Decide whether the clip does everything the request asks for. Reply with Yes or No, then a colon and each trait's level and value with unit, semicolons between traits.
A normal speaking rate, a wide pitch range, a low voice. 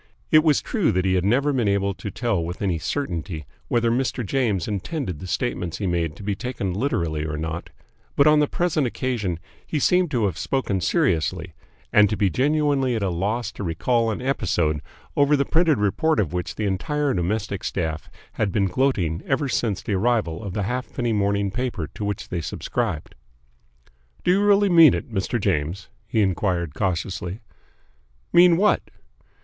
Yes: average, 180 wpm; wide, 6.7 semitones; low, 105 Hz